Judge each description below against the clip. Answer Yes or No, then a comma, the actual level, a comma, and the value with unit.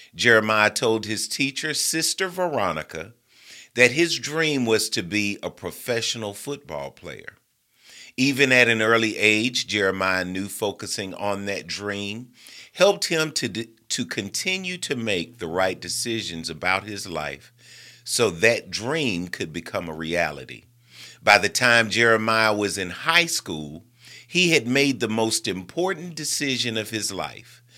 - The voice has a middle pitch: No, low, 115 Hz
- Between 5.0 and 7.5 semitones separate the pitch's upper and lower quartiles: Yes, wide, 5.6 semitones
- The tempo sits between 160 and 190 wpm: No, average, 140 wpm